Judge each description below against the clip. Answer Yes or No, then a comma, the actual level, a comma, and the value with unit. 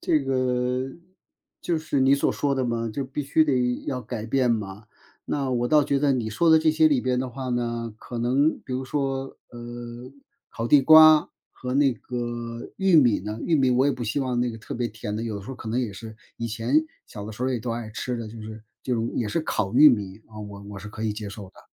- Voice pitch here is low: Yes, low, 125 Hz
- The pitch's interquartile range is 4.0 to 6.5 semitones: No, average, 3.2 semitones